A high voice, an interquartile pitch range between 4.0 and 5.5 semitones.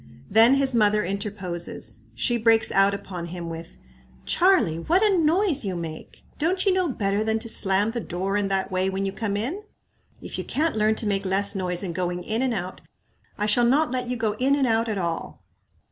Yes: high, 210 Hz; average, 4.7 semitones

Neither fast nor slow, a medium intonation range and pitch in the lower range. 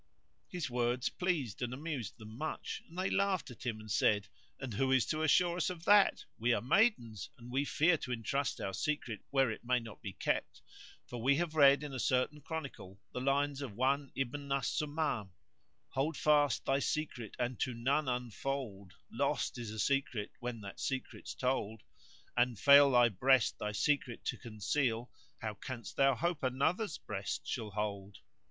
Yes: average, 185 wpm; average, 4.0 semitones; low, 130 Hz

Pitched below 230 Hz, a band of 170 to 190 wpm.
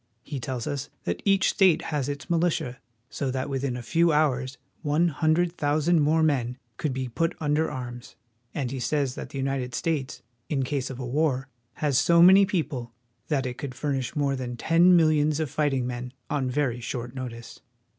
Yes: medium, 140 Hz; average, 185 wpm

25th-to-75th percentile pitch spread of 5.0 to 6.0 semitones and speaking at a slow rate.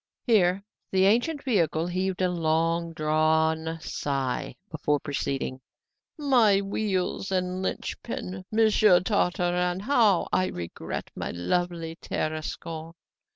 No: average, 3.6 semitones; slow, 105 wpm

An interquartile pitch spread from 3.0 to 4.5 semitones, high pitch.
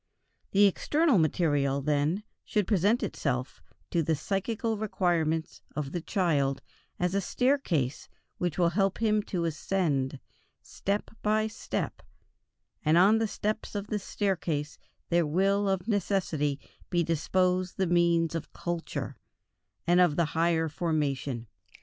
No: average, 4.2 semitones; medium, 175 Hz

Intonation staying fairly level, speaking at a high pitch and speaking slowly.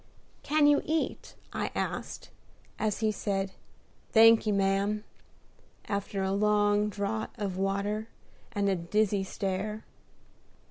Yes: narrow, 1.7 semitones; high, 205 Hz; slow, 110 wpm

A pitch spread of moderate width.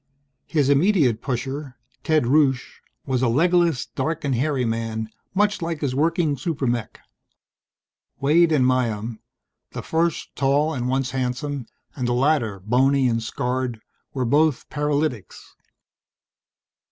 Yes: average, 3.9 semitones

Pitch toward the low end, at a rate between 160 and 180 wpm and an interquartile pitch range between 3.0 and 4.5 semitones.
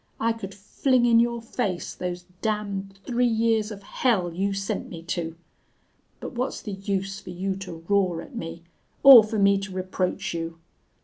No: high, 195 Hz; average, 175 wpm; average, 3.8 semitones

